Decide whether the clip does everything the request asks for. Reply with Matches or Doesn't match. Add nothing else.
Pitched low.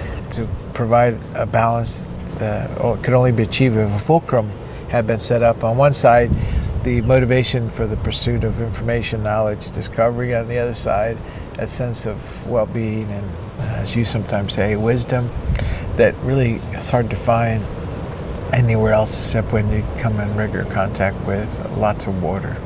Matches